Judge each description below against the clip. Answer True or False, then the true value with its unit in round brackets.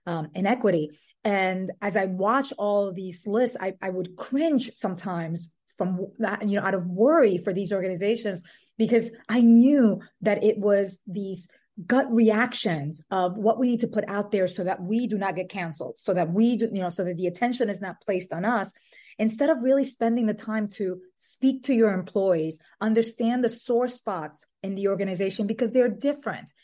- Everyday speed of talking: True (190 wpm)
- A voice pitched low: False (205 Hz)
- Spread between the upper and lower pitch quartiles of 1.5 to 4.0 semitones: True (3.7 semitones)